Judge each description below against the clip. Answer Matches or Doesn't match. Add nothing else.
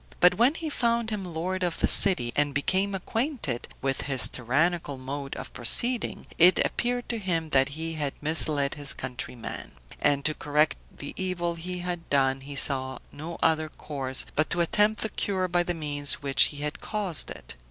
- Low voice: Doesn't match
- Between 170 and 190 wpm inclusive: Matches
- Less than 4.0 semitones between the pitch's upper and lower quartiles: Doesn't match